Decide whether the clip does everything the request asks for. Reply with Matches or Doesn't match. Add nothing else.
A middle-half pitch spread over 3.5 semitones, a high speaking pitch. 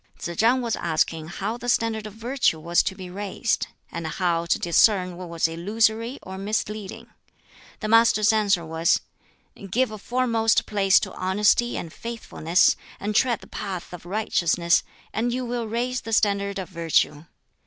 Matches